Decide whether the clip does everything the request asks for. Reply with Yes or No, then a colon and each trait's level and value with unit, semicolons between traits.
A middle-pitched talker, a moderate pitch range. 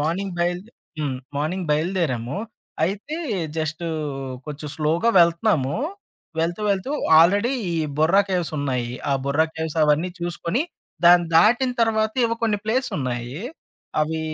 Yes: medium, 170 Hz; average, 4.9 semitones